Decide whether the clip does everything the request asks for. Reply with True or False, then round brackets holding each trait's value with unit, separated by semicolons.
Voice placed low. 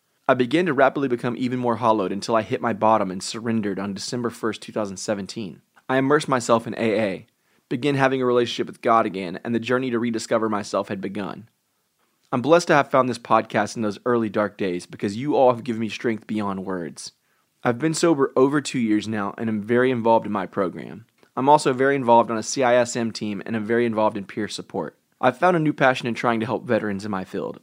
True (115 Hz)